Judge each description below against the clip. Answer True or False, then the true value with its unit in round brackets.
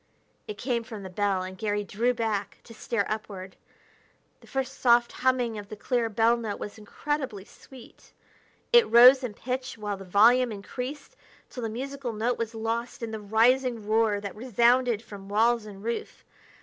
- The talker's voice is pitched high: True (230 Hz)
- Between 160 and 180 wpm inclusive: True (175 wpm)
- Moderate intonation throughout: True (3.2 semitones)